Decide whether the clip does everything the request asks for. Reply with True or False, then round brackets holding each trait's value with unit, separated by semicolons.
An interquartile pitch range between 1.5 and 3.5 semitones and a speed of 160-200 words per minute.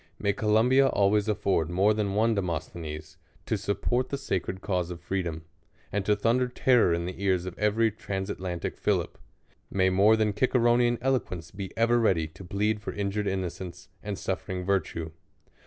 True (3.2 semitones; 170 wpm)